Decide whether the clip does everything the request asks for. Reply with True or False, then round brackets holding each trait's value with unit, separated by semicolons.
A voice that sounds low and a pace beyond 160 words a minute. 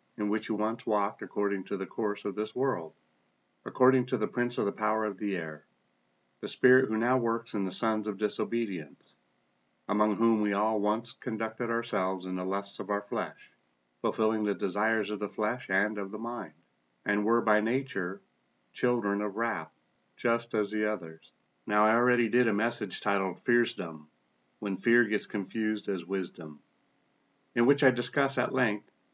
True (105 Hz; 175 wpm)